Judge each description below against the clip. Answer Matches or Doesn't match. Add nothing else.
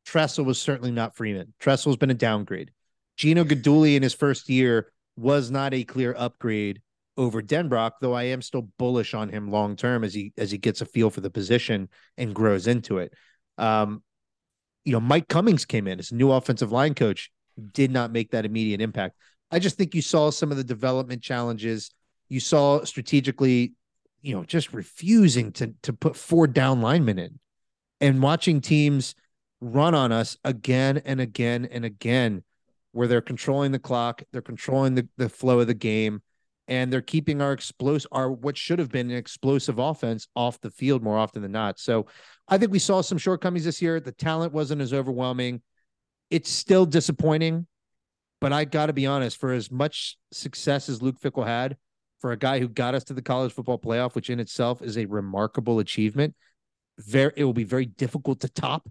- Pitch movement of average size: Matches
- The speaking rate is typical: Matches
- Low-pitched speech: Matches